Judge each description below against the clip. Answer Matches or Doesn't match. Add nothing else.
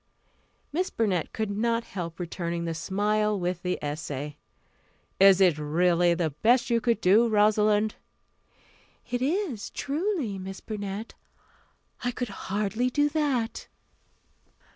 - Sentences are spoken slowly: Matches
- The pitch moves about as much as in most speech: Matches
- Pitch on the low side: Doesn't match